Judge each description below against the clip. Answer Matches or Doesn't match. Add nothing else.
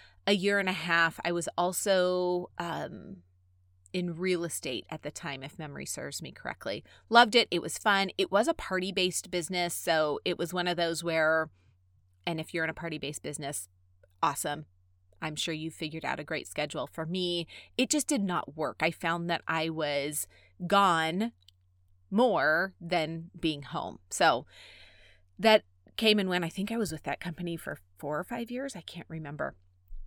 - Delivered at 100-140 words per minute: Doesn't match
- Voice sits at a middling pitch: Matches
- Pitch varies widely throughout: Doesn't match